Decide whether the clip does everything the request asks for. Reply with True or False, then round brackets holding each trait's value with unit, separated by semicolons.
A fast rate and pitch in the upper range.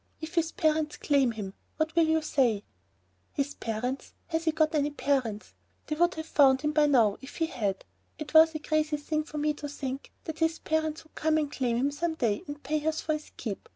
True (220 wpm; 300 Hz)